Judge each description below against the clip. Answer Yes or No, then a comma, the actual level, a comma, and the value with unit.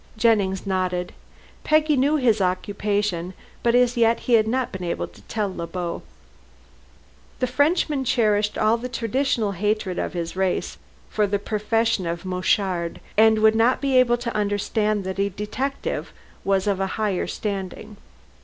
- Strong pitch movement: No, average, 3.7 semitones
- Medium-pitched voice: No, high, 210 Hz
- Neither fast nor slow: Yes, average, 155 wpm